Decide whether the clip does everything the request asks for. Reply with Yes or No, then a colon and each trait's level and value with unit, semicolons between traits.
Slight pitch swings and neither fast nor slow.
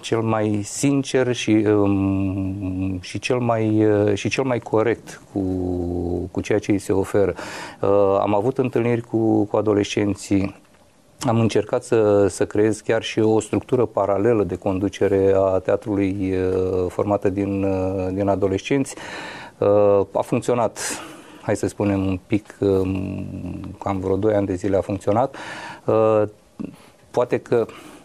Yes: narrow, 2.1 semitones; average, 125 wpm